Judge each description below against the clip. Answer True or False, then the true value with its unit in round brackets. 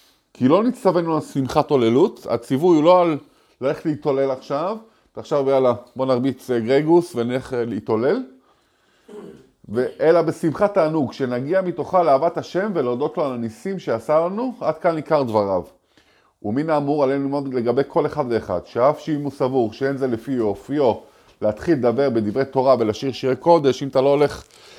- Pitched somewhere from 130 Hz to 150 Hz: True (140 Hz)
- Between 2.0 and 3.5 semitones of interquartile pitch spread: False (4.0 semitones)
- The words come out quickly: True (155 wpm)